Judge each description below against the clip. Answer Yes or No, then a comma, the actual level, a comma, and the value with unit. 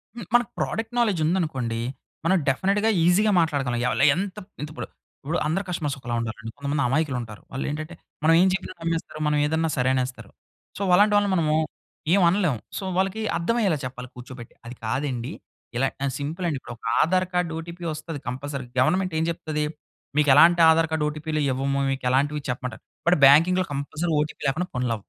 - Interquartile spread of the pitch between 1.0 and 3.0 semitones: No, average, 5.1 semitones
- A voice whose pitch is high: No, medium, 155 Hz